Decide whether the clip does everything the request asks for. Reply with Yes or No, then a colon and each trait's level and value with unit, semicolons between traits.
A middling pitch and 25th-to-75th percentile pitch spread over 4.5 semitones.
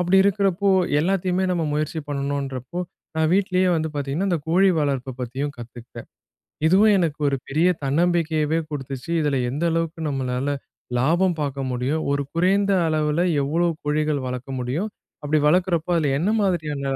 No: medium, 155 Hz; average, 4.2 semitones